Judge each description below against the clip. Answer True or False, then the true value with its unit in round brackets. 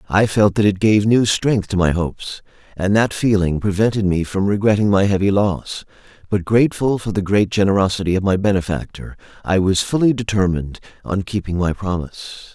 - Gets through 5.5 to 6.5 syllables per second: True (5.6 syllables/s)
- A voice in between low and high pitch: False (100 Hz)